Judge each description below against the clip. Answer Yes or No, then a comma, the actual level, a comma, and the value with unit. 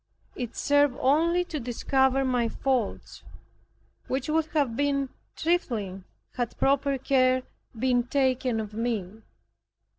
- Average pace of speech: No, slow, 115 wpm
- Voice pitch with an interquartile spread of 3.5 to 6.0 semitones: No, average, 2.9 semitones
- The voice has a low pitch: No, very high, 260 Hz